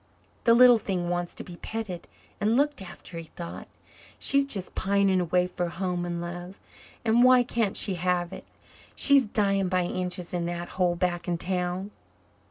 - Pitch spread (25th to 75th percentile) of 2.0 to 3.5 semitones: Yes, average, 3.0 semitones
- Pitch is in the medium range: Yes, medium, 180 Hz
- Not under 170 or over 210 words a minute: Yes, average, 175 wpm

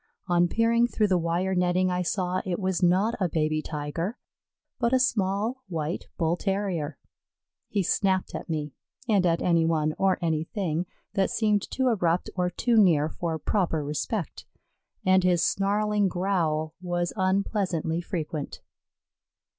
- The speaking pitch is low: No, medium, 180 Hz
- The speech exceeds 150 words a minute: No, average, 145 wpm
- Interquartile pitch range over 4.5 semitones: No, average, 3.3 semitones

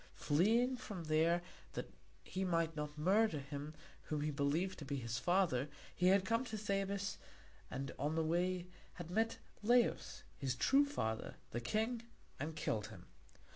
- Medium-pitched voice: Yes, medium, 170 Hz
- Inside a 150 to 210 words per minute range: Yes, average, 160 wpm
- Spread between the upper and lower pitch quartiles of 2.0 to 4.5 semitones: No, wide, 5.4 semitones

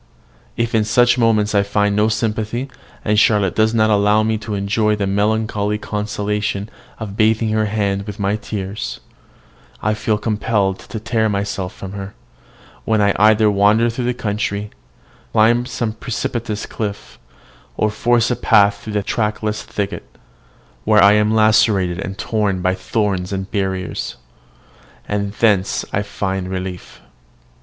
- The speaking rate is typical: Yes, average, 150 wpm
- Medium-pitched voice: No, low, 105 Hz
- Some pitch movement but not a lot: No, narrow, 1.5 semitones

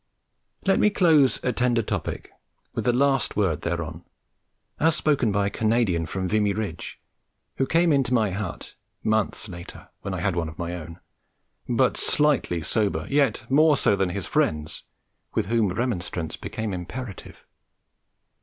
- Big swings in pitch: Yes, wide, 6.6 semitones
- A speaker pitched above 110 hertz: No, low, 105 Hz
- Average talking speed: Yes, average, 155 wpm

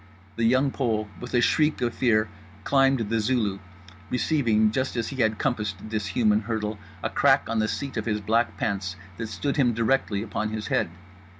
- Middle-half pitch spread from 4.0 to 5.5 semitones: No, average, 2.8 semitones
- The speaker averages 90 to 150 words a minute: No, average, 185 wpm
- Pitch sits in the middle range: No, low, 110 Hz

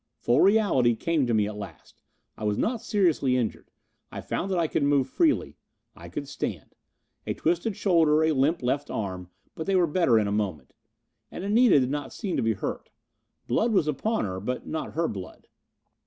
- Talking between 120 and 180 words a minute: No, average, 195 wpm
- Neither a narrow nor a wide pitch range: No, wide, 8.2 semitones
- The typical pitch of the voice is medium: Yes, medium, 145 Hz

